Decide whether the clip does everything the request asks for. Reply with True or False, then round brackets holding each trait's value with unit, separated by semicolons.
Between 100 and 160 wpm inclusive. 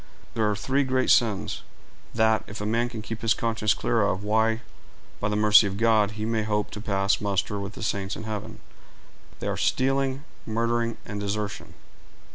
False (185 wpm)